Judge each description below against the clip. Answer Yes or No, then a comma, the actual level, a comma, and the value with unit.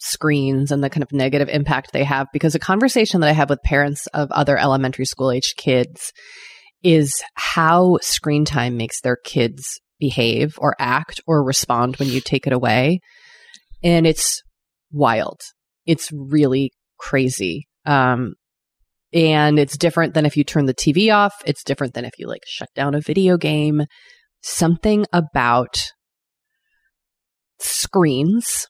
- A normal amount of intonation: Yes, average, 3.7 semitones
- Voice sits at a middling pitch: Yes, medium, 145 Hz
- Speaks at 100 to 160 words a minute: Yes, average, 150 wpm